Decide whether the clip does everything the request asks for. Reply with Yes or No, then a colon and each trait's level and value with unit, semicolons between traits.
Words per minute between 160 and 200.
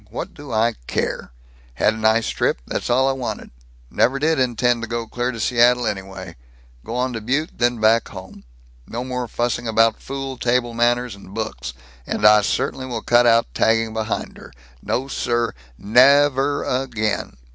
Yes: average, 170 wpm